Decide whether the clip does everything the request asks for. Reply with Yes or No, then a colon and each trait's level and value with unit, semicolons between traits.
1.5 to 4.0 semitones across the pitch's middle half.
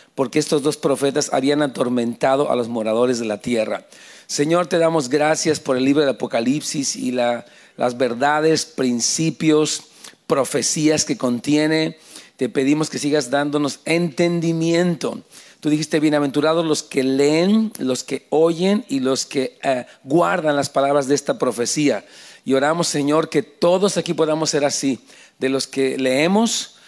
Yes: average, 3.2 semitones